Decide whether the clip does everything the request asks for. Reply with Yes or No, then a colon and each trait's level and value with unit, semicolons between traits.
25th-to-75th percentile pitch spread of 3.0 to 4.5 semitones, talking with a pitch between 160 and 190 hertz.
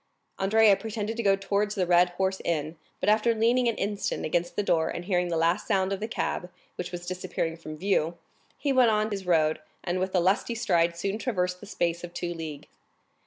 Yes: average, 3.4 semitones; medium, 185 Hz